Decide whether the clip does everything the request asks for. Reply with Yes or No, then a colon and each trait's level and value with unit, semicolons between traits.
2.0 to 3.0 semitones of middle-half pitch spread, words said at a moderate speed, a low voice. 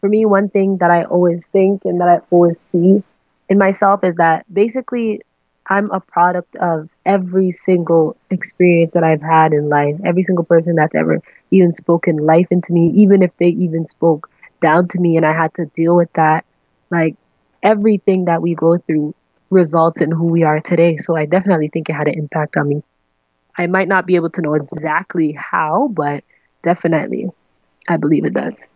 No: narrow, 2.6 semitones; average, 190 wpm; medium, 170 Hz